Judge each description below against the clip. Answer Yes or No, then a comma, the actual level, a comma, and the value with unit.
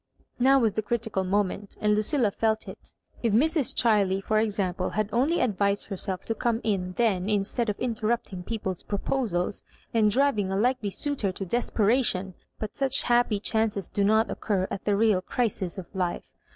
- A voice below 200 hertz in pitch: No, high, 210 Hz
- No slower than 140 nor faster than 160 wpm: No, average, 175 wpm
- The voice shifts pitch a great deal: No, average, 3.2 semitones